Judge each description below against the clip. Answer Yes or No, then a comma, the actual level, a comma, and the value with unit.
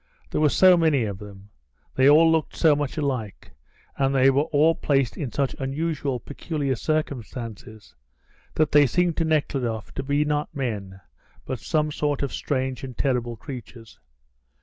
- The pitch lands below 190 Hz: Yes, medium, 140 Hz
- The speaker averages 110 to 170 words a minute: Yes, average, 160 wpm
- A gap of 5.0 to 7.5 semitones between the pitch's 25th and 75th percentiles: No, average, 3.6 semitones